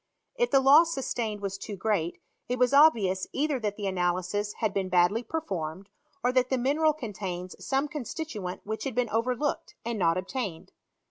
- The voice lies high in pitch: Yes, high, 220 Hz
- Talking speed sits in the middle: Yes, average, 175 wpm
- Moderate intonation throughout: No, wide, 5.9 semitones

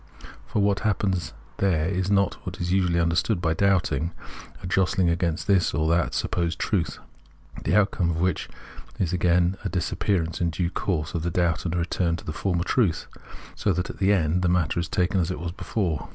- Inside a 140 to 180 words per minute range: No, average, 200 wpm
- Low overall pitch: Yes, very low, 90 Hz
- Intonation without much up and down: Yes, narrow, 2.1 semitones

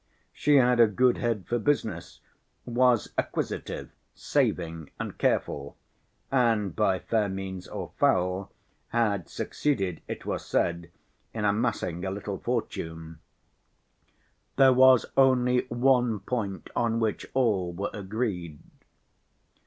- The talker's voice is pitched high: No, low, 105 Hz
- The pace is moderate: No, slow, 115 wpm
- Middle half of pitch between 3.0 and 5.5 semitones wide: Yes, average, 4.8 semitones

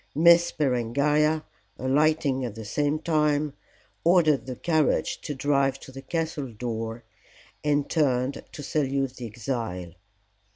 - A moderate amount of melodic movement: Yes, average, 3.5 semitones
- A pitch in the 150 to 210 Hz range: No, medium, 140 Hz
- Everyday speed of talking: No, slow, 125 wpm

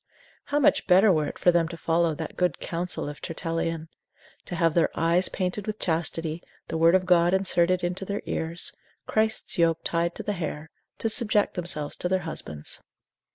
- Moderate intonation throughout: No, narrow, 2.0 semitones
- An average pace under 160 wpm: No, average, 185 wpm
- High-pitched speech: No, medium, 170 Hz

